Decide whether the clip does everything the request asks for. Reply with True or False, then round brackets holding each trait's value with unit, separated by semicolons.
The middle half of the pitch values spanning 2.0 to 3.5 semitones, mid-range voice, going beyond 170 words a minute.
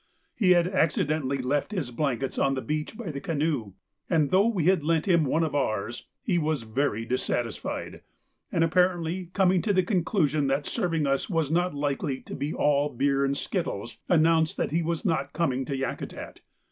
False (4.1 semitones; 155 Hz; 185 wpm)